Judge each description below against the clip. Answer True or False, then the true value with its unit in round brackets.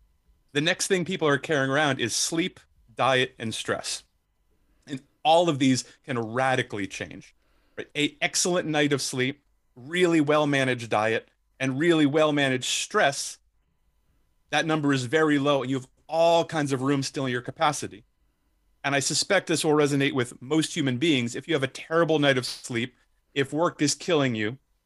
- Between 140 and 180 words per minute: True (175 wpm)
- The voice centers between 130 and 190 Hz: True (140 Hz)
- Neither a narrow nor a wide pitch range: True (3.4 semitones)